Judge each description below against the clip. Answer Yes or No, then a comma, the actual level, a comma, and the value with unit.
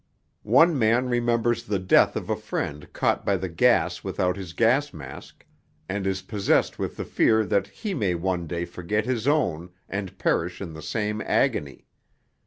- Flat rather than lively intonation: No, average, 4.8 semitones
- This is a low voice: Yes, low, 100 Hz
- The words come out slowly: No, average, 175 wpm